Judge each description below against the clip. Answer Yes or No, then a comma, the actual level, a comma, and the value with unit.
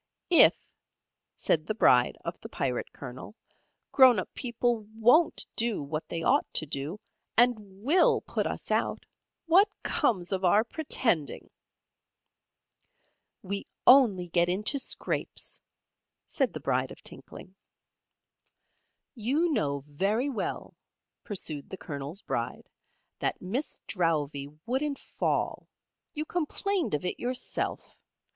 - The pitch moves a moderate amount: No, wide, 8.0 semitones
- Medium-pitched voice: No, high, 210 Hz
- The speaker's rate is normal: No, slow, 120 wpm